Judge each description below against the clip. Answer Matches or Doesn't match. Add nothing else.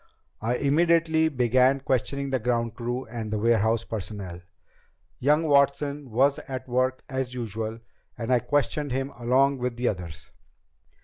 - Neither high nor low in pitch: Doesn't match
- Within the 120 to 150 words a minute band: Matches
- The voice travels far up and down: Doesn't match